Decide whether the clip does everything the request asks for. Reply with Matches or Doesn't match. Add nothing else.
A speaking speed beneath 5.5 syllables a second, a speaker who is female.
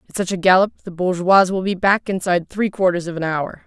Doesn't match